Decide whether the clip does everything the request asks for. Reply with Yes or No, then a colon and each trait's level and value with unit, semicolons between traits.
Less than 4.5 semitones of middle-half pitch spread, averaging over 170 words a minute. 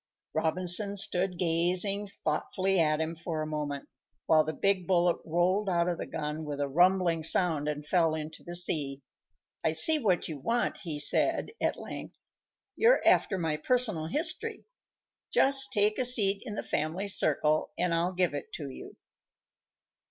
No: average, 3.8 semitones; average, 165 wpm